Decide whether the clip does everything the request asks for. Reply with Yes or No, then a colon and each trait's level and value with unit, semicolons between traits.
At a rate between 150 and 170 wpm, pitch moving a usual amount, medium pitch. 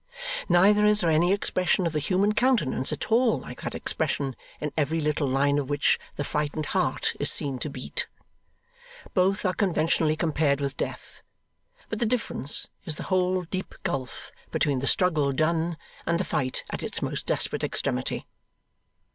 Yes: average, 165 wpm; average, 4.5 semitones; medium, 160 Hz